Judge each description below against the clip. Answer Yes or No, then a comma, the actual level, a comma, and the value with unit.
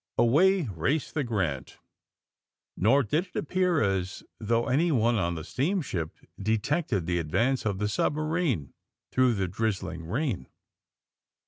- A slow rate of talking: Yes, slow, 125 wpm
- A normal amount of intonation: No, wide, 7.8 semitones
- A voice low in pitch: Yes, low, 115 Hz